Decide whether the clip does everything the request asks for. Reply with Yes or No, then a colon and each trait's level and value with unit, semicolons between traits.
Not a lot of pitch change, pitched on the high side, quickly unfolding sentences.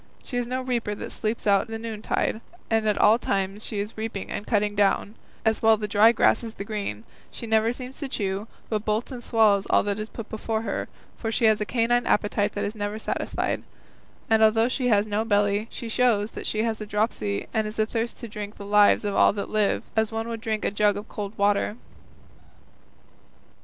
Yes: narrow, 1.6 semitones; high, 215 Hz; fast, 210 wpm